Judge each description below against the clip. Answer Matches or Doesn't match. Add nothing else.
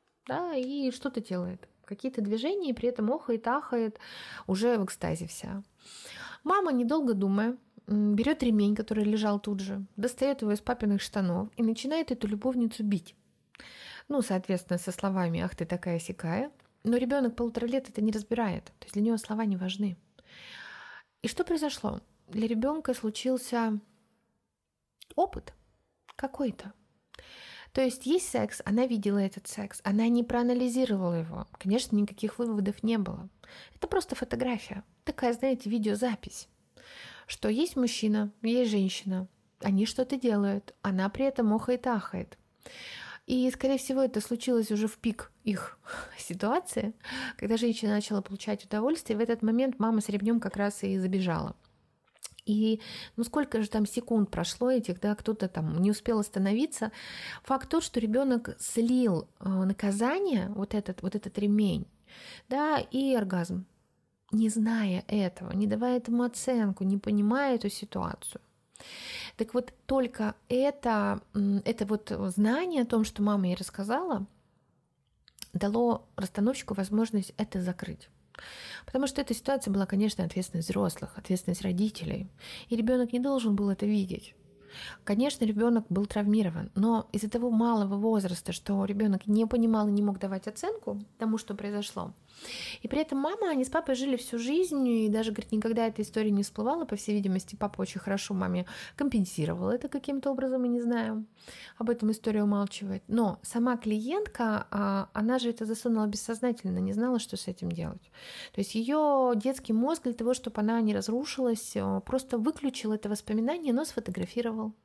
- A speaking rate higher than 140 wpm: Matches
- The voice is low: Doesn't match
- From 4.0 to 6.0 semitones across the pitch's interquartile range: Doesn't match